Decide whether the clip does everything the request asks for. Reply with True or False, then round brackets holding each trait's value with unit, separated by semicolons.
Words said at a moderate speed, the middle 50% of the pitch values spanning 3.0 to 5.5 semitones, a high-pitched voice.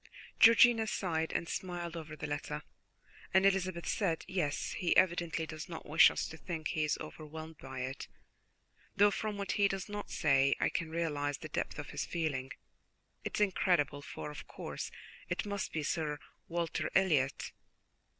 False (170 wpm; 3.9 semitones; 165 Hz)